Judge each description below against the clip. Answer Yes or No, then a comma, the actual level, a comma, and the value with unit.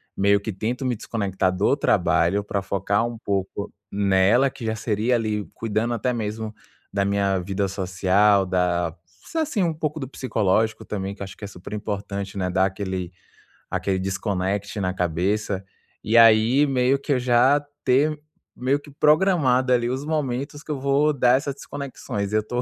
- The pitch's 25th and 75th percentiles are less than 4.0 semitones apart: No, average, 4.8 semitones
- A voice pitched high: No, low, 110 Hz